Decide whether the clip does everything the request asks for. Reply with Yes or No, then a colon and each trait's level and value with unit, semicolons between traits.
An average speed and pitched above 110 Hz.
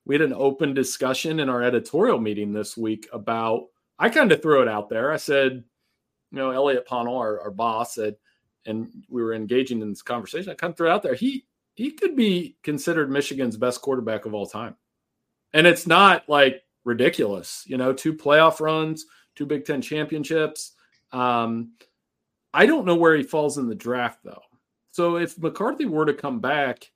Yes: average, 190 wpm; low, 135 Hz